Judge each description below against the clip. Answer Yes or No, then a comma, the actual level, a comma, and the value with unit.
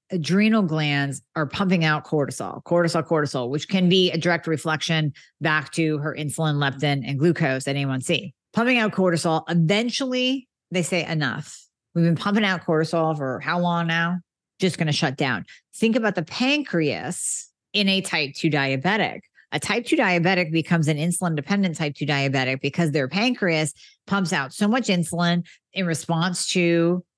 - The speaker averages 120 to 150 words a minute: No, average, 170 wpm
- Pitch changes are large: No, average, 3.5 semitones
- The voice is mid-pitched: Yes, medium, 170 Hz